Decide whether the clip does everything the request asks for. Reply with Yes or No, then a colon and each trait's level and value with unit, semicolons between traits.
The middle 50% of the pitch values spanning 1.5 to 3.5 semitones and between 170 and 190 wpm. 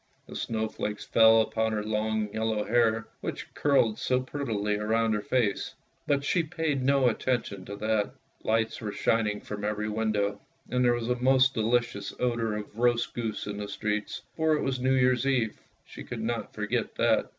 Yes: average, 2.8 semitones; average, 185 wpm